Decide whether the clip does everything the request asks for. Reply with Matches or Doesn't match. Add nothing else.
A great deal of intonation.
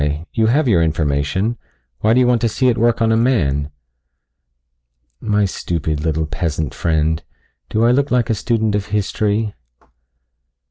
Matches